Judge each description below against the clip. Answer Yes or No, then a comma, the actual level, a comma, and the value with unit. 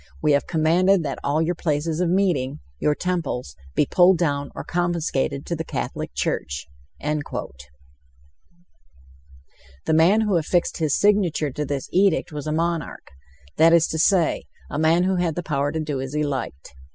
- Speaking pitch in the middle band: Yes, medium, 155 Hz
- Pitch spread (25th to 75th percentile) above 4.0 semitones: Yes, average, 4.6 semitones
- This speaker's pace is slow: No, average, 165 wpm